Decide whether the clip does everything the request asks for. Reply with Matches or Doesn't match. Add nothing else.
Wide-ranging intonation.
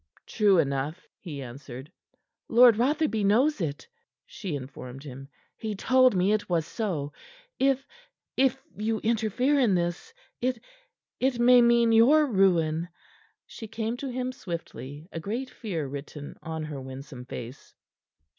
Matches